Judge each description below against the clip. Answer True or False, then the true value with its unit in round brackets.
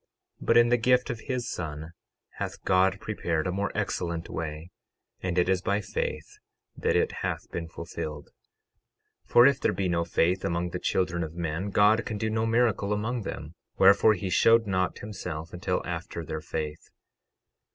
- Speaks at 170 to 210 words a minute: True (175 wpm)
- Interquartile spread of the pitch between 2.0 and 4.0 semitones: False (4.4 semitones)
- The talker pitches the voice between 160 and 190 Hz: False (95 Hz)